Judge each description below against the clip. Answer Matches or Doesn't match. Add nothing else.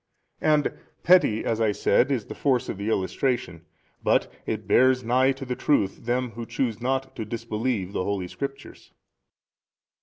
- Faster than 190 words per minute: Doesn't match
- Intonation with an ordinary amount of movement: Matches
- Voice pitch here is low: Matches